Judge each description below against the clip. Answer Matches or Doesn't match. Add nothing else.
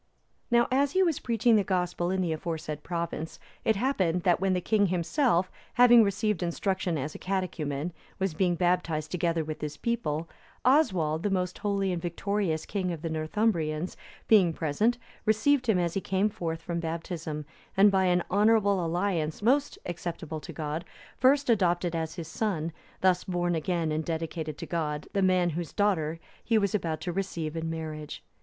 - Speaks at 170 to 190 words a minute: Matches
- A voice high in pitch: Doesn't match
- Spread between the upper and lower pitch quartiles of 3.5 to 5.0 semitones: Matches